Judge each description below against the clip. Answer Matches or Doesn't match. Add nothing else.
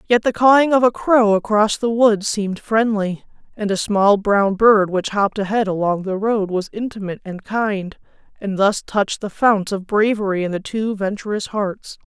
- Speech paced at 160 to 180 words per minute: Doesn't match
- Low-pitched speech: Doesn't match